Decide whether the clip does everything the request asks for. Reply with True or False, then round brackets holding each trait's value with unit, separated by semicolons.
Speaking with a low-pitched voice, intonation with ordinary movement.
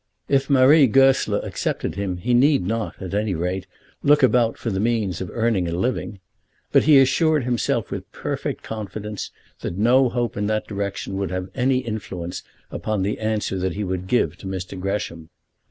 True (105 Hz; 4.7 semitones)